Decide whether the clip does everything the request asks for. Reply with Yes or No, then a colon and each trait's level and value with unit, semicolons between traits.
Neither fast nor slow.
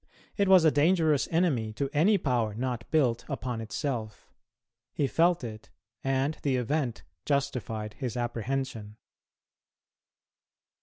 No: slow, 115 wpm